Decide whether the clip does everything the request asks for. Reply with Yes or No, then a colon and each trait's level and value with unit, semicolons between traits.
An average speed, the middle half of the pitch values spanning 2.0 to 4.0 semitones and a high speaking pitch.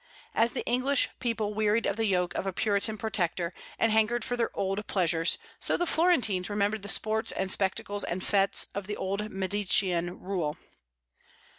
Yes: average, 170 wpm; average, 2.7 semitones; high, 205 Hz